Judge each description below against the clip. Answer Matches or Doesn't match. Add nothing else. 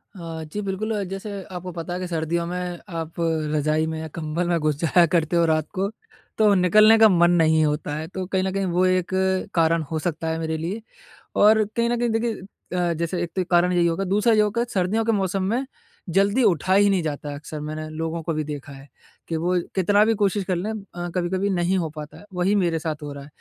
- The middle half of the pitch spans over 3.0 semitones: Matches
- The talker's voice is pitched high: Doesn't match